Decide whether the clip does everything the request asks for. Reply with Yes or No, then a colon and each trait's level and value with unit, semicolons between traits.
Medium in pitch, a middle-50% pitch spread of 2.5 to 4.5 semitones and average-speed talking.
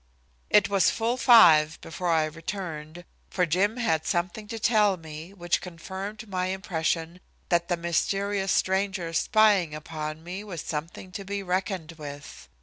Yes: medium, 180 Hz; average, 3.6 semitones; average, 145 wpm